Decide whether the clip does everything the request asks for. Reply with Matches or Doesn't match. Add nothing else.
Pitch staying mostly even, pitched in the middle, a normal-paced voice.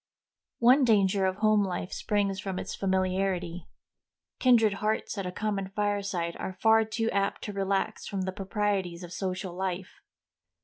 Doesn't match